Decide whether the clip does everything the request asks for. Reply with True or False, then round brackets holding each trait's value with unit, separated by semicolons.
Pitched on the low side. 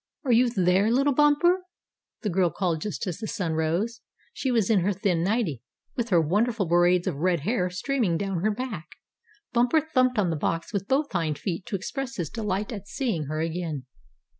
False (195 Hz)